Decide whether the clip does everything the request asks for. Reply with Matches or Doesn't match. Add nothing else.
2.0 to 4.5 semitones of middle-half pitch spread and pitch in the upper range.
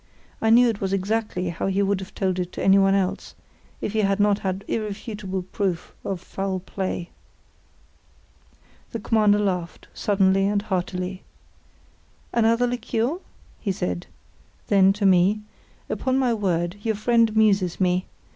Matches